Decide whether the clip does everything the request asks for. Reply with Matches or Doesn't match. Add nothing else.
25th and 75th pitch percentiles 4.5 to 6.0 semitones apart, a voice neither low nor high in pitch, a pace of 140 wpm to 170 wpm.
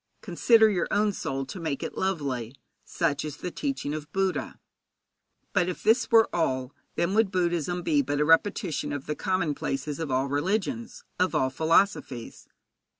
Matches